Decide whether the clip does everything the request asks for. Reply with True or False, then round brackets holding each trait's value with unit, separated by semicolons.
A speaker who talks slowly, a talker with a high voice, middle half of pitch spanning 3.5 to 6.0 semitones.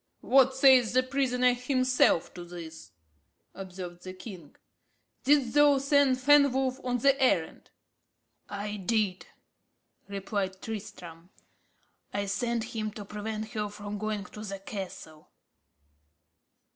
True (115 wpm; 215 Hz; 4.8 semitones)